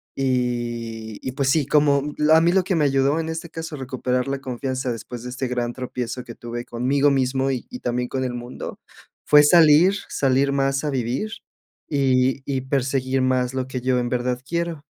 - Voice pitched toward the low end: Yes, low, 130 Hz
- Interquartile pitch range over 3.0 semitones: No, narrow, 2.5 semitones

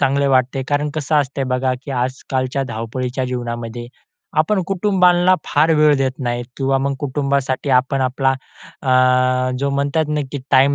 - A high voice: No, low, 135 Hz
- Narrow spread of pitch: Yes, narrow, 2.2 semitones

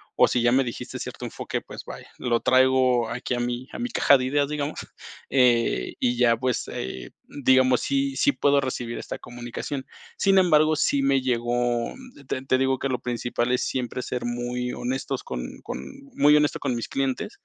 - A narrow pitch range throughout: Yes, narrow, 2.2 semitones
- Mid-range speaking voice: No, low, 125 Hz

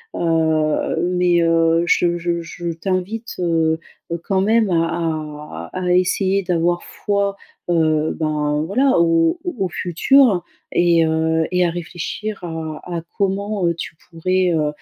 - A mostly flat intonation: Yes, narrow, 2.3 semitones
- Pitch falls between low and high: Yes, medium, 170 Hz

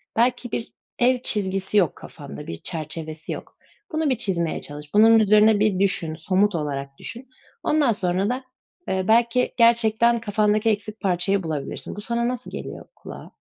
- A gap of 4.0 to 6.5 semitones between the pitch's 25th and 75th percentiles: Yes, average, 4.9 semitones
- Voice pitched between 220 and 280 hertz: No, high, 210 Hz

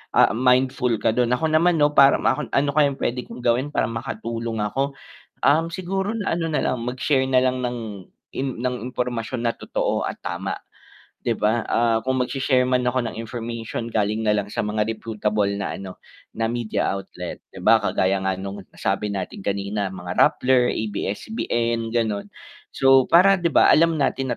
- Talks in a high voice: No, low, 120 Hz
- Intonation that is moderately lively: Yes, average, 3.8 semitones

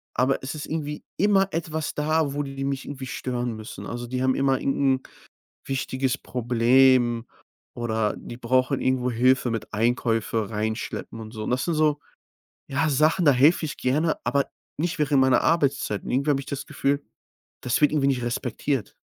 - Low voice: Yes, low, 130 Hz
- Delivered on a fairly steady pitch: No, average, 3.2 semitones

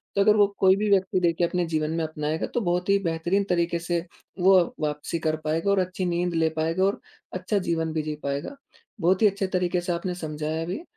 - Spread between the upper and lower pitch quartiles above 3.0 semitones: No, average, 2.7 semitones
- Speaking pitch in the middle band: Yes, medium, 175 Hz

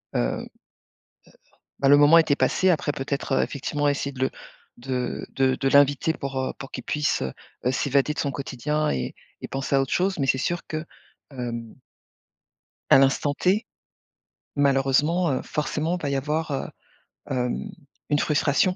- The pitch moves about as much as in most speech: No, narrow, 2.2 semitones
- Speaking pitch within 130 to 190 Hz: Yes, medium, 140 Hz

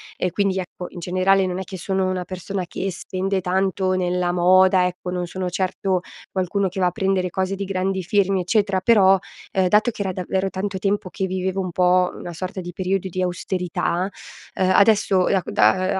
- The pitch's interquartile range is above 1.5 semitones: No, narrow, 1.1 semitones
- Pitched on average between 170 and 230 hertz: Yes, medium, 185 Hz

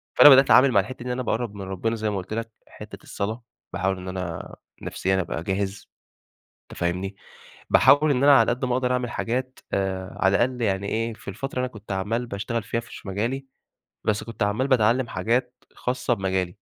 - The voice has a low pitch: Yes, low, 115 Hz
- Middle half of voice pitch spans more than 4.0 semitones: Yes, average, 4.4 semitones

